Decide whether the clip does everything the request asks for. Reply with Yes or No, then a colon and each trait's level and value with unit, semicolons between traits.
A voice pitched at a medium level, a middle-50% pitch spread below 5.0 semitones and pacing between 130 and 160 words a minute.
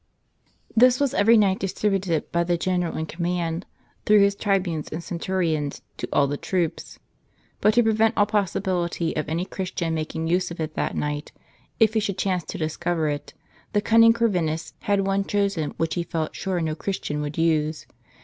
No: medium, 180 Hz; average, 3.7 semitones; average, 180 wpm